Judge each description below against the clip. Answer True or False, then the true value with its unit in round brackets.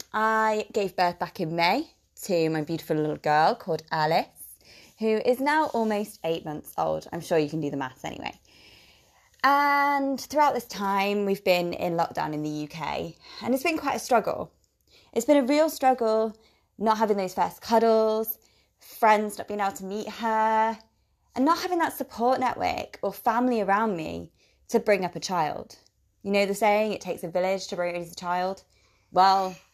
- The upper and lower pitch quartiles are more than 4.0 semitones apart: True (5.1 semitones)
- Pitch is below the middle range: False (205 Hz)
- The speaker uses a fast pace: False (180 wpm)